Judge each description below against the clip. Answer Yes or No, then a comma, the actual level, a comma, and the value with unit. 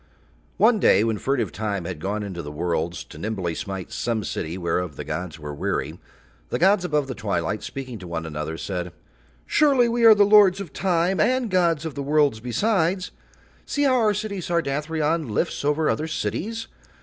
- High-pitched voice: No, medium, 140 Hz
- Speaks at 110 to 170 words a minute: No, average, 185 wpm